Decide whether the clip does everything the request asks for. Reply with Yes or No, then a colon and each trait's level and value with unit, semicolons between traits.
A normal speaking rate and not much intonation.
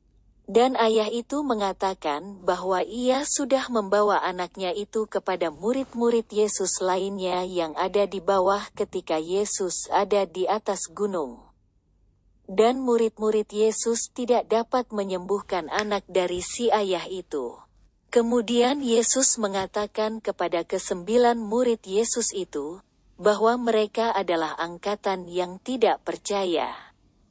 No: average, 110 wpm; average, 3.9 semitones